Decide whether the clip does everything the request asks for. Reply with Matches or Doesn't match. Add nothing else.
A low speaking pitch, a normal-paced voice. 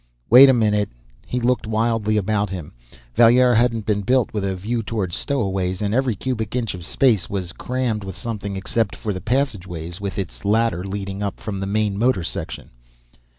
Matches